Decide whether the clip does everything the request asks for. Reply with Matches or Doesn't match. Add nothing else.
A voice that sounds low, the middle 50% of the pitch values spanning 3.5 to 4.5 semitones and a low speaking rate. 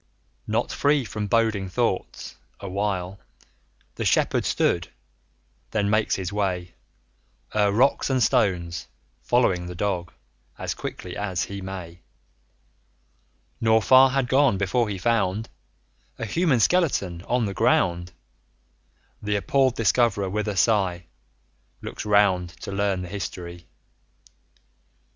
Matches